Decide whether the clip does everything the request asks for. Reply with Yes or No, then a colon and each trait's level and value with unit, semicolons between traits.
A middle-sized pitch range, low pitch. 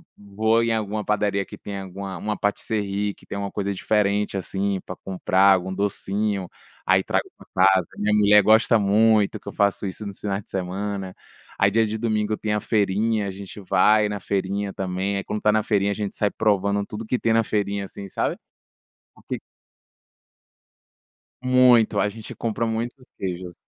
No: narrow, 1.6 semitones; low, 100 Hz